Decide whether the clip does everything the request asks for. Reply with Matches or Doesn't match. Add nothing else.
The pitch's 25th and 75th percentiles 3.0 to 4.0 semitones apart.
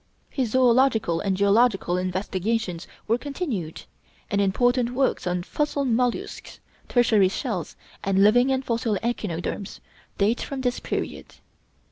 Doesn't match